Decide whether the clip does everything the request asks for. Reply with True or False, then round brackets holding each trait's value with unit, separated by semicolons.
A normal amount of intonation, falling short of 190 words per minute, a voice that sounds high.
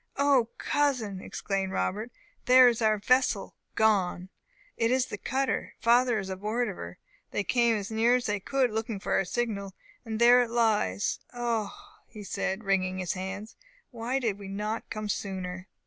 True (3.6 semitones; 175 wpm; 220 Hz)